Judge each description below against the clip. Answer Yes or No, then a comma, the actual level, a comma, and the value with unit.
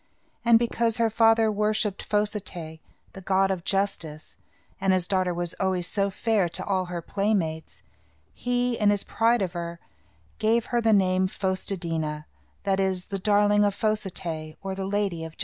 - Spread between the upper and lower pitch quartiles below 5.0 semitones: Yes, average, 3.0 semitones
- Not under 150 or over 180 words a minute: No, average, 195 wpm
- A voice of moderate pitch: No, high, 195 Hz